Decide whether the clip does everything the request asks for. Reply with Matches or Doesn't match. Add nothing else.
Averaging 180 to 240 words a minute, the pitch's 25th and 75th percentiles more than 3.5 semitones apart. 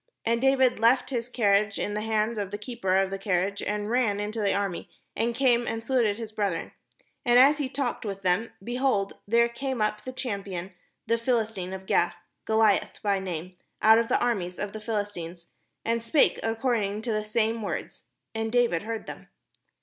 Doesn't match